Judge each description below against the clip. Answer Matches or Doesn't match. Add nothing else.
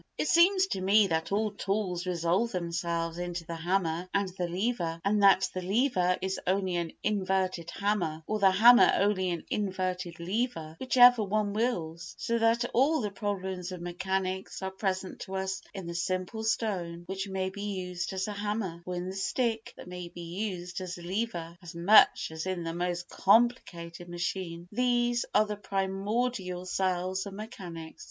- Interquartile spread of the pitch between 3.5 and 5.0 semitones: Doesn't match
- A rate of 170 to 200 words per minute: Matches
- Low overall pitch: Doesn't match